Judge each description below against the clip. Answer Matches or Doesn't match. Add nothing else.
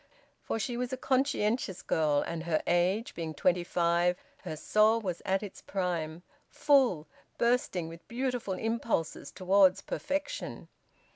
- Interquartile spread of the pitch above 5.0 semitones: Matches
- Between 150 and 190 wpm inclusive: Doesn't match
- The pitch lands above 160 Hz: Matches